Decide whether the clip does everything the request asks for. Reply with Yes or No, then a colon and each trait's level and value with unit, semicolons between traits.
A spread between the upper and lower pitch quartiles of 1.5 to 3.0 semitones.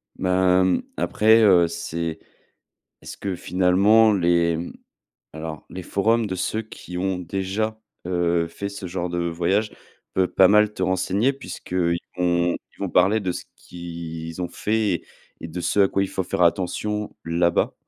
Yes: average, 2.7 semitones